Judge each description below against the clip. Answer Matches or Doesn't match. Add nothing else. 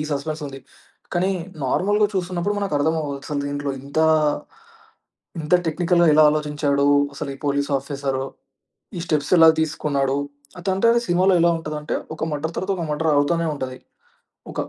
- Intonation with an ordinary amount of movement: Matches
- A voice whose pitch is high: Doesn't match